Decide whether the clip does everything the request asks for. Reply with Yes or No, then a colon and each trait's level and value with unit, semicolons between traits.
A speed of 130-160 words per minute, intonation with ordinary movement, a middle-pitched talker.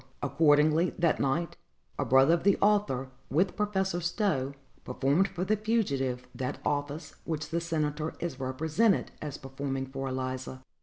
Yes: average, 145 wpm; average, 4.6 semitones; medium, 150 Hz